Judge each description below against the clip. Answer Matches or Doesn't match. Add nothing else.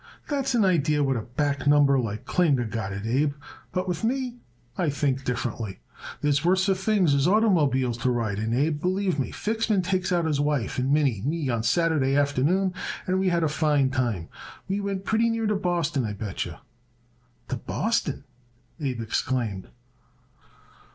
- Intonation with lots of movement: Matches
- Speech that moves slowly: Doesn't match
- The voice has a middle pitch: Matches